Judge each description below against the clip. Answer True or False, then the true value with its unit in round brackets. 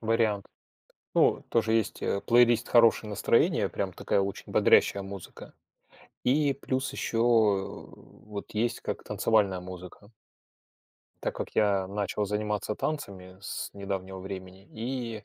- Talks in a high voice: False (105 Hz)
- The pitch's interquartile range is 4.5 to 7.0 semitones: False (2.8 semitones)